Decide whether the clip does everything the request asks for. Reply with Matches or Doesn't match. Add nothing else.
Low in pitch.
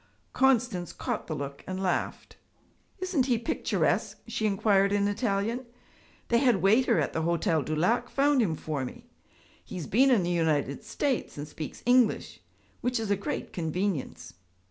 Doesn't match